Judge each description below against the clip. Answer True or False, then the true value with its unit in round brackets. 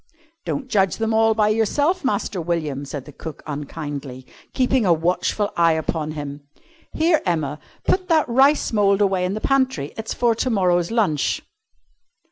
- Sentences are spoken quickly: False (155 wpm)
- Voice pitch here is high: True (195 Hz)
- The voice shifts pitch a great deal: True (7.0 semitones)